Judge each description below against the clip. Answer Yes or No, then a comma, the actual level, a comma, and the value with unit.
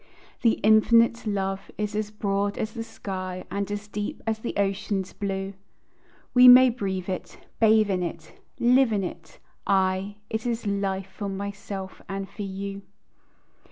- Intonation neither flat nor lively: No, narrow, 2.1 semitones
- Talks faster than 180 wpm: No, average, 155 wpm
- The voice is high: Yes, high, 200 Hz